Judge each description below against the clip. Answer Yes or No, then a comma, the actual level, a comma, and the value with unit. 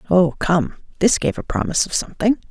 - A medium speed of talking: Yes, average, 190 wpm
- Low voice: No, high, 195 Hz